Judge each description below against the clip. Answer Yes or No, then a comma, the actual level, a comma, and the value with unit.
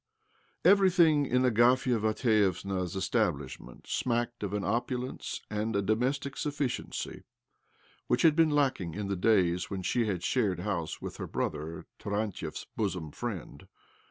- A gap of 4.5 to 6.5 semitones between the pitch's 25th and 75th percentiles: Yes, average, 5.1 semitones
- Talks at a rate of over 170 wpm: No, average, 140 wpm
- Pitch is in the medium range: No, low, 110 Hz